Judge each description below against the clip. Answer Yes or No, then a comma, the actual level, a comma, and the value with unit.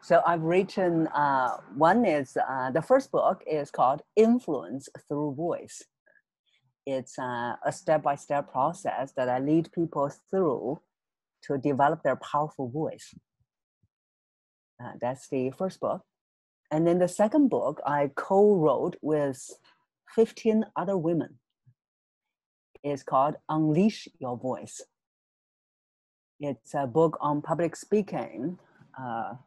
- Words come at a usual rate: No, slow, 120 wpm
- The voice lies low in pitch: No, medium, 150 Hz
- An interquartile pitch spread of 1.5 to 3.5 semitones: No, average, 4.2 semitones